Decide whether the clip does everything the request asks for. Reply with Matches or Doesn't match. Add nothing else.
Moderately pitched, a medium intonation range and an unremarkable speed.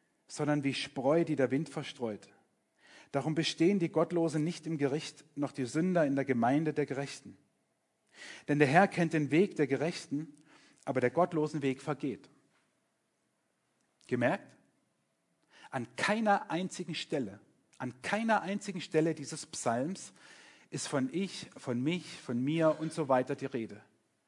Matches